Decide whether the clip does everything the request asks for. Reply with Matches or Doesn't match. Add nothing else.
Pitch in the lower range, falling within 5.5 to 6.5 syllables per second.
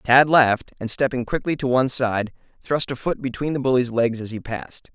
Matches